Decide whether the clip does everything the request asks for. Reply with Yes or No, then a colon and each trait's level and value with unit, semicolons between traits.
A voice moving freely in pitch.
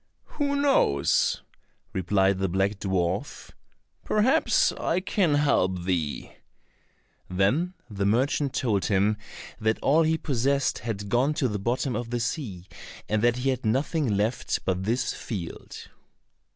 Yes: wide, 6.5 semitones